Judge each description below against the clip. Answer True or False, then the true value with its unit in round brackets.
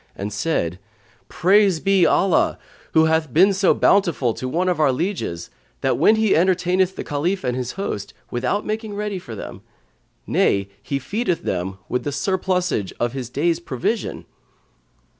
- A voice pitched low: False (170 Hz)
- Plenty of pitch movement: True (7.3 semitones)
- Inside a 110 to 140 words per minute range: False (155 wpm)